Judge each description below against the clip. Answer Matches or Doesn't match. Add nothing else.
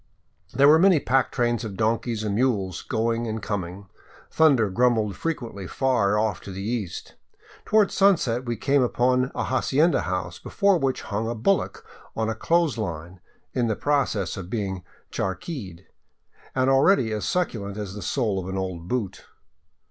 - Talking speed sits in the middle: Matches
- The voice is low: Matches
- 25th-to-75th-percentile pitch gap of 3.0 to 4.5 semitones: Doesn't match